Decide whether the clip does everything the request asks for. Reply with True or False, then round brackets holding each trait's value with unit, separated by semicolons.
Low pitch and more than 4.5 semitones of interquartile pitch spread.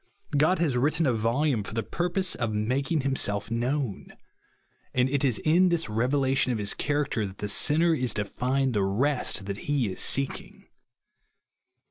True (130 Hz; 5.1 semitones)